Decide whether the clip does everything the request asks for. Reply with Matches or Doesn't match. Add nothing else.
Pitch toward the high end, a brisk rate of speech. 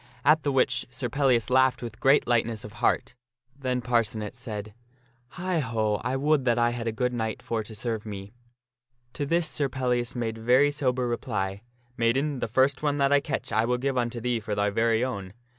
Doesn't match